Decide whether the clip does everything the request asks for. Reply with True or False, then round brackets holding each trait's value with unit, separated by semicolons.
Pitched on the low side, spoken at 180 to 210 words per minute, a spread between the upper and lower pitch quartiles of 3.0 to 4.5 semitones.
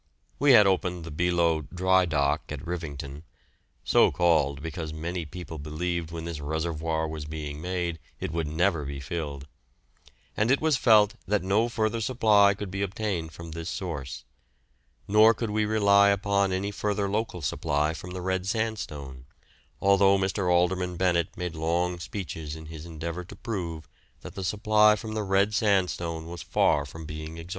False (90 Hz; 165 wpm; 4.0 semitones)